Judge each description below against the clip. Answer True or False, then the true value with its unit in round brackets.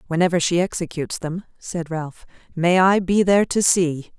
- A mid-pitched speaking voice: True (175 Hz)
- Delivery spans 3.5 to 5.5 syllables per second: True (5.1 syllables/s)